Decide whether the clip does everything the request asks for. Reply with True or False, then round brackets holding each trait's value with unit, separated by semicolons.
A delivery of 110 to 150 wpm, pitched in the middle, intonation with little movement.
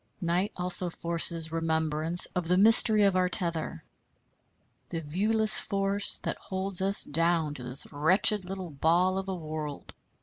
False (145 wpm; 175 Hz; 3.2 semitones)